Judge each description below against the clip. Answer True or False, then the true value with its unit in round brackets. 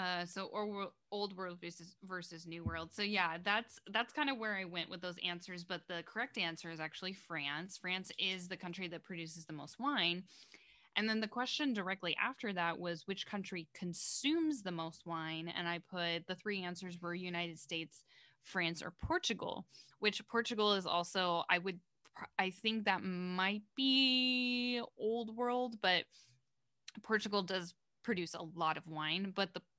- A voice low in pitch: False (185 Hz)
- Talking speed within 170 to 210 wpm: True (175 wpm)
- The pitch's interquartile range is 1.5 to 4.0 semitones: True (3.7 semitones)